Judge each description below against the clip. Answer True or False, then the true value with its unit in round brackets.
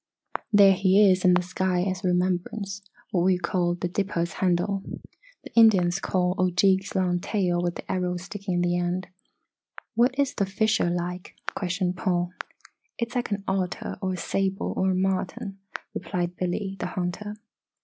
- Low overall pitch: False (185 Hz)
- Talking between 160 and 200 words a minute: True (165 wpm)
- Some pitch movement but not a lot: False (1.7 semitones)